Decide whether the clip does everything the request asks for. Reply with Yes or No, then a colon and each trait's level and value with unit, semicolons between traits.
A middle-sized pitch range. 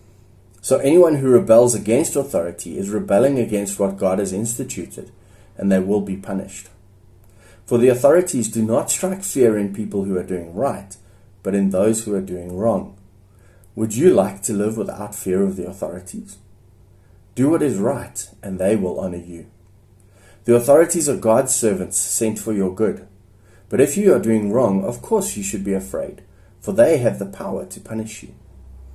Yes: average, 3.0 semitones